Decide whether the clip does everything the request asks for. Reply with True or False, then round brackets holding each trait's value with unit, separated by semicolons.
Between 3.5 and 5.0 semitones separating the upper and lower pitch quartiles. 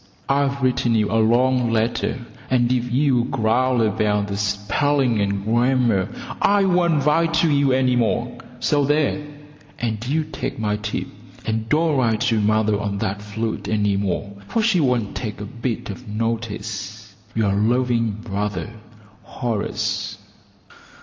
True (3.8 semitones)